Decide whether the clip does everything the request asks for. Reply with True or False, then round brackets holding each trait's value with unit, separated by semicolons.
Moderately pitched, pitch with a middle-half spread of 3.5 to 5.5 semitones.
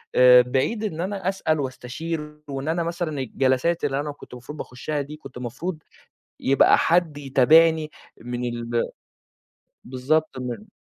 True (145 Hz; 4.3 semitones)